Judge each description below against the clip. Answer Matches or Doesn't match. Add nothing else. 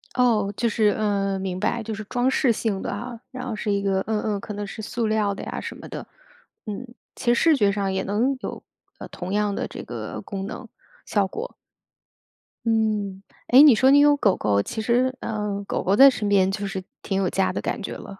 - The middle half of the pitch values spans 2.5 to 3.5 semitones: Matches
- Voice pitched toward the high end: Matches